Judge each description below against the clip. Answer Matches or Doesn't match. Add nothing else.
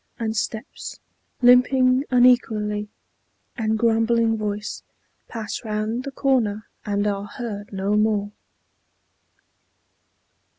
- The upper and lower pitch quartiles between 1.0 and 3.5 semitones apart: Matches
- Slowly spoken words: Matches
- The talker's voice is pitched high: Matches